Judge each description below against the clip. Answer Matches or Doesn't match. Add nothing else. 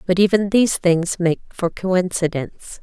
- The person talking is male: Doesn't match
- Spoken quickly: Doesn't match